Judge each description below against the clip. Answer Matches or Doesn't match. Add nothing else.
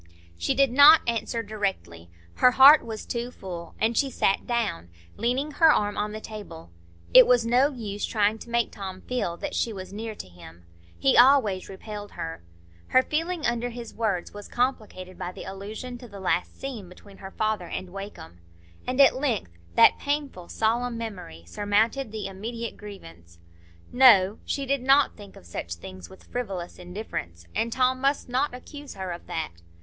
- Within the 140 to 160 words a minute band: Doesn't match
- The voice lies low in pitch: Doesn't match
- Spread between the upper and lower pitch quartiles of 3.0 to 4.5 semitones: Doesn't match